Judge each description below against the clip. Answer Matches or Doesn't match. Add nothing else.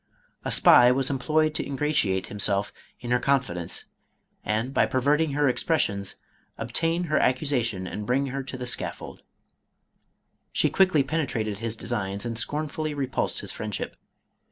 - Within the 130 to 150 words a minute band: Matches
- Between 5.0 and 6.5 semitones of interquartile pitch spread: Matches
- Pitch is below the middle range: Matches